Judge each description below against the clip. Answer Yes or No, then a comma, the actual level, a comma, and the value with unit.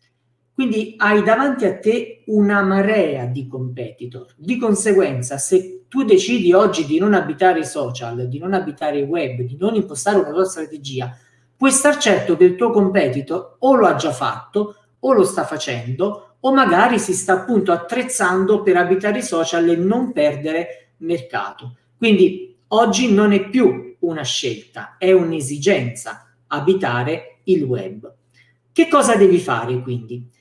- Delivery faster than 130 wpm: Yes, average, 155 wpm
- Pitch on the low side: No, medium, 185 Hz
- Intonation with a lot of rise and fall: Yes, wide, 7.3 semitones